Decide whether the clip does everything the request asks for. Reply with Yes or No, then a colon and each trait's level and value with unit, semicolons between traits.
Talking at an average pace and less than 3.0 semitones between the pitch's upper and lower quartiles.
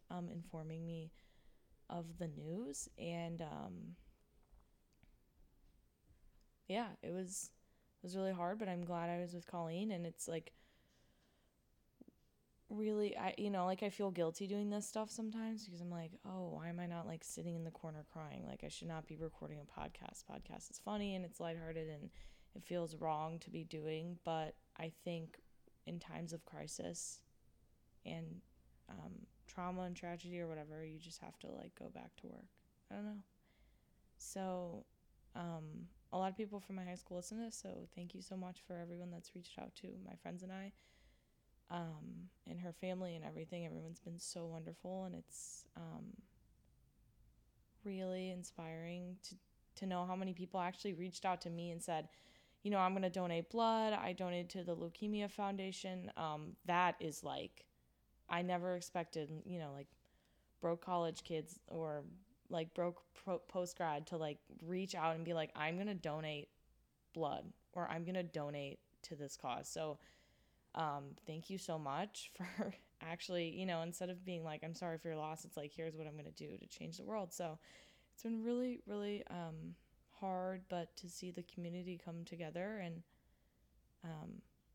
Yes: average, 180 wpm; narrow, 2.5 semitones